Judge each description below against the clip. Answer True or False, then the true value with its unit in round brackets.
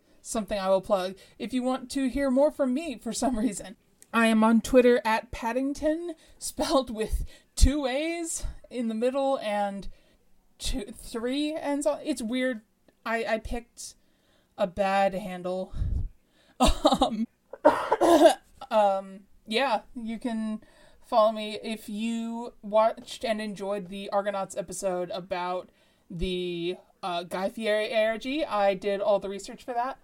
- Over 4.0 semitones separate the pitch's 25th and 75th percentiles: True (4.5 semitones)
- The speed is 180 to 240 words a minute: False (140 wpm)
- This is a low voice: False (225 Hz)